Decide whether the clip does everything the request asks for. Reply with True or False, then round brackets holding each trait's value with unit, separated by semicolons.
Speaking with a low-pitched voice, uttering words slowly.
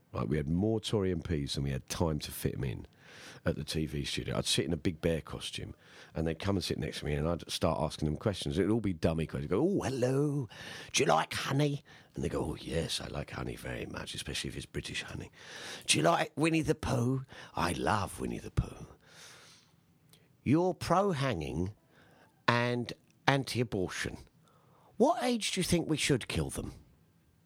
False (105 Hz; 205 wpm)